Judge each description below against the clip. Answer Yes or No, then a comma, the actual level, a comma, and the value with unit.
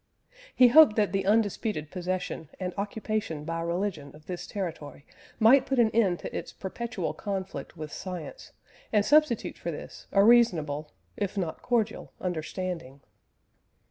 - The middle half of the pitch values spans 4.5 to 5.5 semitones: Yes, average, 4.8 semitones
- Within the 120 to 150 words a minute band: Yes, average, 140 wpm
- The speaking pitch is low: No, high, 190 Hz